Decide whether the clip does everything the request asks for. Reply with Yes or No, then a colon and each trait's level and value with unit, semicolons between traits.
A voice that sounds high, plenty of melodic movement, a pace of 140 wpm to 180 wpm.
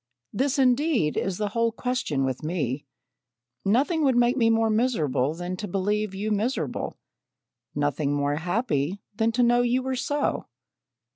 Yes: high, 215 Hz; wide, 7.4 semitones; average, 150 wpm